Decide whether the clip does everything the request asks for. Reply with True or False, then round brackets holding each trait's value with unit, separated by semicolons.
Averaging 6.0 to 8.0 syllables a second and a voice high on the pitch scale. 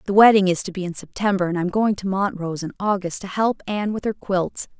True (6.1 syllables/s; 195 Hz)